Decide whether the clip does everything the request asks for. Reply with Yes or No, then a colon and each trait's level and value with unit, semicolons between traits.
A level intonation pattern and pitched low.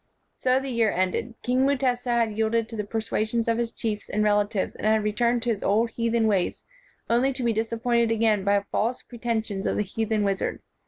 No: narrow, 2.0 semitones; high, 225 Hz